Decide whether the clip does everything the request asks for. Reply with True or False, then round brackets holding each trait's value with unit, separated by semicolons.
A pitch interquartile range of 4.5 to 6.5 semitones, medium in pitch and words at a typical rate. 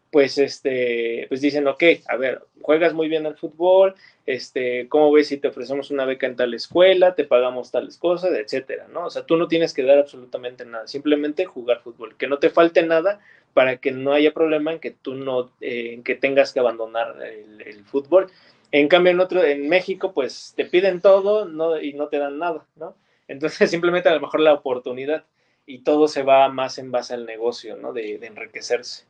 False (4.9 semitones; 150 Hz; 210 wpm)